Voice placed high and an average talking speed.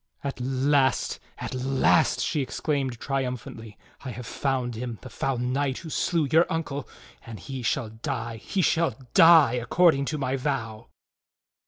No: low, 135 Hz; average, 150 wpm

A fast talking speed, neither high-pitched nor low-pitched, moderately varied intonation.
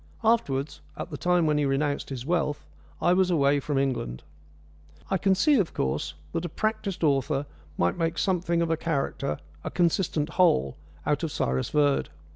No: average, 175 wpm; medium, 155 Hz; average, 4.3 semitones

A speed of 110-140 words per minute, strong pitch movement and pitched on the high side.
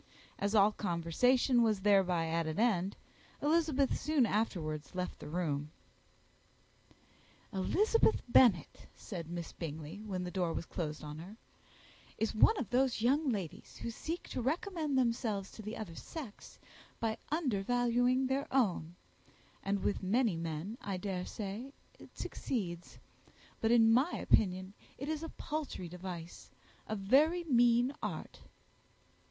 Yes: slow, 135 wpm; wide, 6.2 semitones; high, 215 Hz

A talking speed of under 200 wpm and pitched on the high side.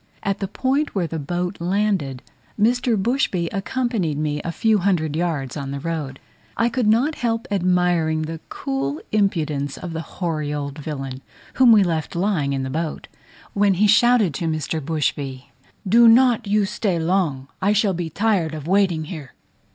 No: average, 170 wpm; medium, 175 Hz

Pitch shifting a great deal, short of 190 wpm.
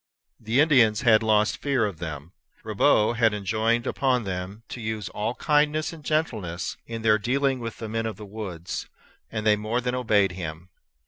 No: average, 3.3 semitones; average, 180 wpm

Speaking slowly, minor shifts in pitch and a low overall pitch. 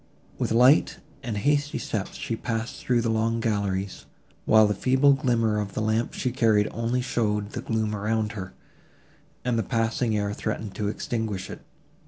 No: average, 170 wpm; narrow, 2.2 semitones; low, 110 Hz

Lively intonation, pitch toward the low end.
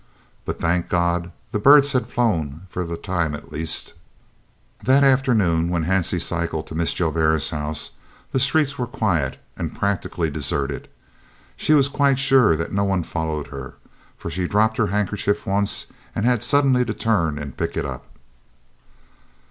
Yes: wide, 6.9 semitones; very low, 90 Hz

